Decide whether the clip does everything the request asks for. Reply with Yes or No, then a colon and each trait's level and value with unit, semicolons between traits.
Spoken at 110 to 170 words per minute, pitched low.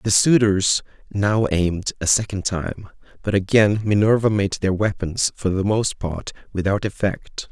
Yes: average, 150 wpm; low, 100 Hz